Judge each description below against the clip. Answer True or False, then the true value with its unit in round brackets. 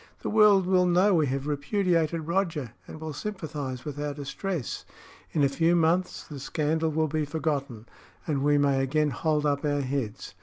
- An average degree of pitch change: True (3.0 semitones)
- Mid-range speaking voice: True (150 Hz)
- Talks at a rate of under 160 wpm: False (180 wpm)